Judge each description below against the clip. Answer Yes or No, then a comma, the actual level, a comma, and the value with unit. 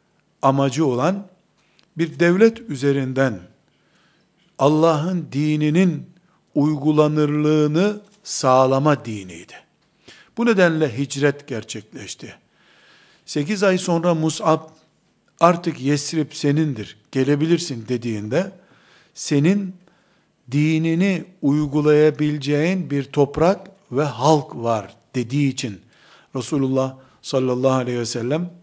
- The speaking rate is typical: No, slow, 80 wpm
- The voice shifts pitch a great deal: No, average, 4.1 semitones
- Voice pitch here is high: No, medium, 150 Hz